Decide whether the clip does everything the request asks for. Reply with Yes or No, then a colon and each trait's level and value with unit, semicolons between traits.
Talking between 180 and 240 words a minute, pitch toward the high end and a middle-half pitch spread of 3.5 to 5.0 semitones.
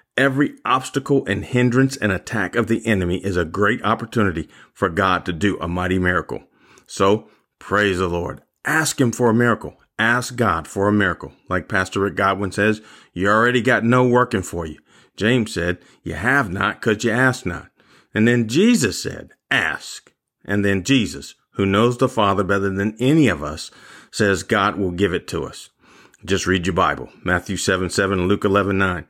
No: average, 185 wpm; low, 100 Hz; average, 4.1 semitones